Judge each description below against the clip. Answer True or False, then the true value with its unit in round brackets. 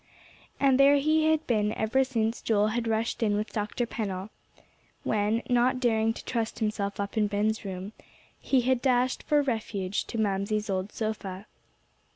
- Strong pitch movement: False (3.1 semitones)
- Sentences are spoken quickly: False (165 wpm)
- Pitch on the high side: True (220 Hz)